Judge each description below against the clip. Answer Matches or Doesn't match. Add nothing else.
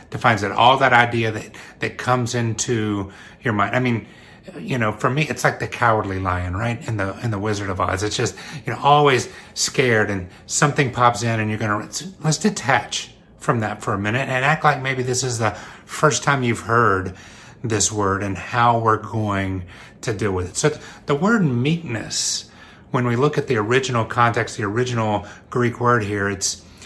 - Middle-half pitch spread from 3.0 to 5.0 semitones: Matches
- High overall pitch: Doesn't match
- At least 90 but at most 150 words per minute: Doesn't match